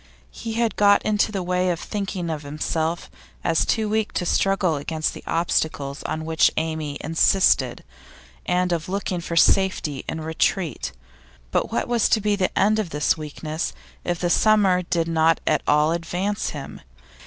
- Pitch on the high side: No, medium, 170 Hz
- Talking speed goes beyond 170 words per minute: No, average, 165 wpm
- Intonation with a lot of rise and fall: No, average, 3.7 semitones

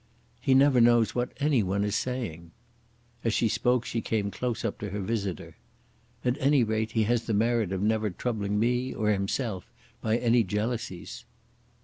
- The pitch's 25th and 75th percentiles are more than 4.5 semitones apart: No, average, 2.9 semitones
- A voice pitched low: Yes, low, 110 Hz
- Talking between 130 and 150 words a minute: No, average, 170 wpm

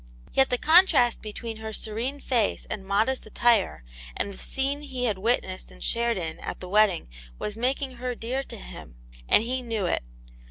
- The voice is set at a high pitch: Yes, high, 230 Hz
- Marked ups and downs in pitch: No, average, 3.8 semitones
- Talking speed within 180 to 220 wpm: Yes, average, 185 wpm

